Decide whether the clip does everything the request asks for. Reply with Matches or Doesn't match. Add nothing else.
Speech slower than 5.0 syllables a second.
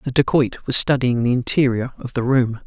Doesn't match